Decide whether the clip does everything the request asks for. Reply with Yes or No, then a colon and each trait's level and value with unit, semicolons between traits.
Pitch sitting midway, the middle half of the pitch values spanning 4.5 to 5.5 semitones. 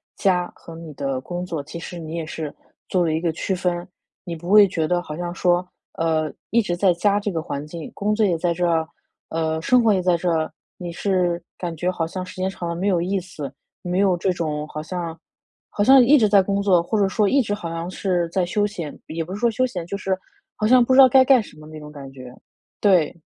No: medium, 175 Hz; average, 3.3 semitones